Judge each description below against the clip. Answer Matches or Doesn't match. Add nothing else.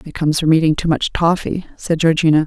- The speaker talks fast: Matches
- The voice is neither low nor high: Matches